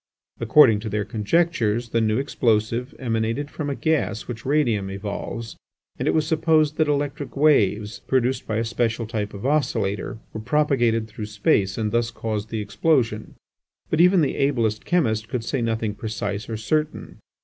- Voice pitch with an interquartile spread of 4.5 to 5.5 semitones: Yes, average, 4.9 semitones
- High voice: No, low, 115 Hz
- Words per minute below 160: No, average, 165 wpm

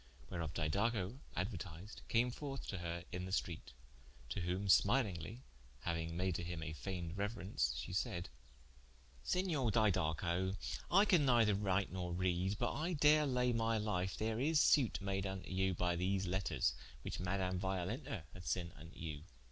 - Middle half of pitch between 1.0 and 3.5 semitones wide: No, average, 4.5 semitones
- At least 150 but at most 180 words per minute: Yes, average, 160 wpm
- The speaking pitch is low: Yes, very low, 95 Hz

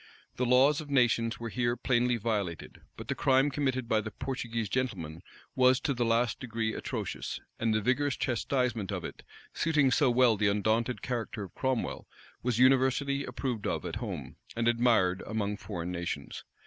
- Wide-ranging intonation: No, average, 3.0 semitones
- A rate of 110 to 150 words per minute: No, average, 170 wpm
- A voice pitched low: Yes, low, 120 Hz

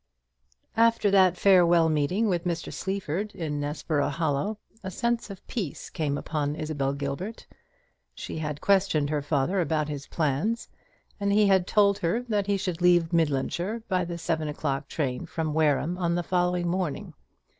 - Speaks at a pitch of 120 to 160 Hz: No, medium, 170 Hz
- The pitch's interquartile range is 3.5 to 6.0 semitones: Yes, average, 4.5 semitones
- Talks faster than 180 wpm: No, average, 160 wpm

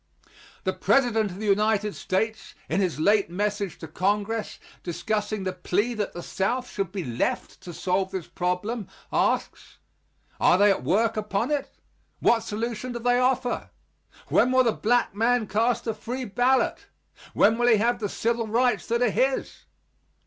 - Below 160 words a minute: No, average, 165 wpm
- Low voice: No, high, 215 Hz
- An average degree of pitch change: Yes, average, 3.5 semitones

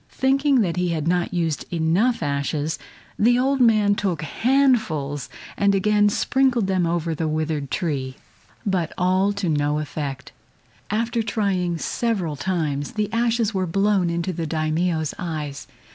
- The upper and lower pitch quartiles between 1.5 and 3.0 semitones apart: No, average, 5.2 semitones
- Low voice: No, medium, 180 Hz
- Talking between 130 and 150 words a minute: Yes, average, 145 wpm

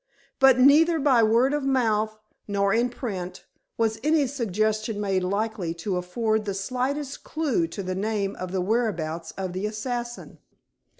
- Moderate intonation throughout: Yes, average, 4.5 semitones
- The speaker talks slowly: No, average, 155 wpm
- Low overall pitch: No, high, 215 Hz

